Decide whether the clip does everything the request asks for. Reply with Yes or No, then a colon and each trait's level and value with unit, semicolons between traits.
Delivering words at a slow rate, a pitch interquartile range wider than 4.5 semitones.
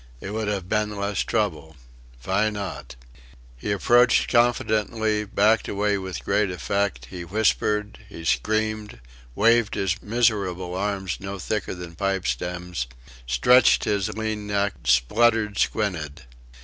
No: slow, 125 wpm; average, 3.2 semitones